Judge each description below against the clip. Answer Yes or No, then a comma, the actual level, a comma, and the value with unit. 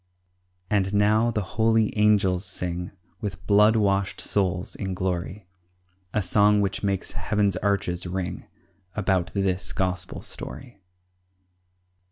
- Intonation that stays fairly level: Yes, narrow, 2.3 semitones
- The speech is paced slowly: Yes, slow, 115 wpm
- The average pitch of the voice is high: No, low, 100 Hz